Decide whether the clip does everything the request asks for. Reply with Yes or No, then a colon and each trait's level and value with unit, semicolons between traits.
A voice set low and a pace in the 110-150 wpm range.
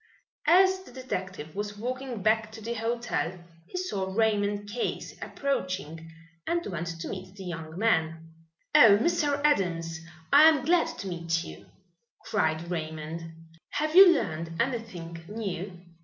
No: high, 205 Hz; average, 140 wpm